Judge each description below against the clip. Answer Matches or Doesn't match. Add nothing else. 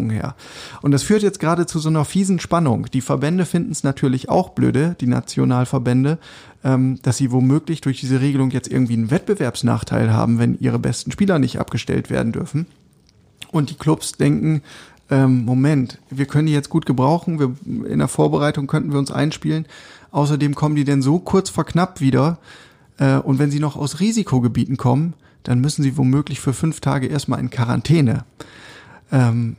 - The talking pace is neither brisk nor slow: Matches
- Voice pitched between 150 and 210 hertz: Doesn't match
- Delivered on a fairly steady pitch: Doesn't match